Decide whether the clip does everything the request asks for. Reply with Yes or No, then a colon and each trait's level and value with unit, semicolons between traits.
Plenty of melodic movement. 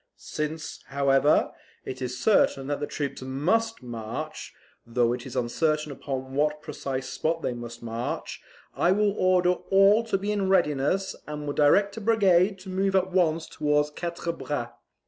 Yes: wide, 5.9 semitones